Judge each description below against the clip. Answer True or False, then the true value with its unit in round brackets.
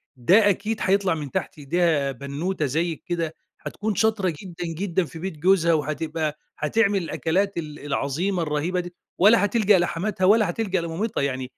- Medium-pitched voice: True (175 Hz)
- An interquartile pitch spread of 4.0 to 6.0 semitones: True (4.3 semitones)